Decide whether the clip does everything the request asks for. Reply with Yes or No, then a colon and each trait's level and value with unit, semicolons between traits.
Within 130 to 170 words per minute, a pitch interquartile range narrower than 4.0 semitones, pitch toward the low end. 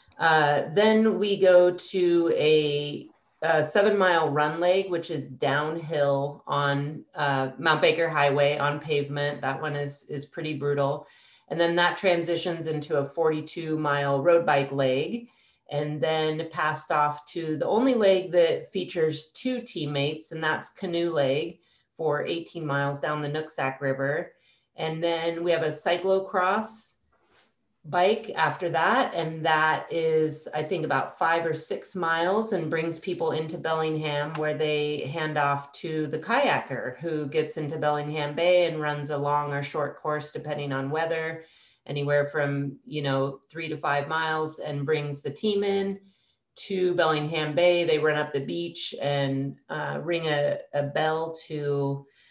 No: average, 155 wpm; average, 2.7 semitones; medium, 155 Hz